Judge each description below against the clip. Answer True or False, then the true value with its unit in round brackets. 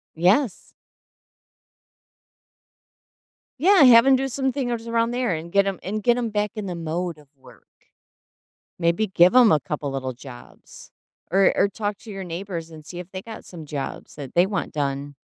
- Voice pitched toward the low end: False (190 Hz)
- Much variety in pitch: True (6.2 semitones)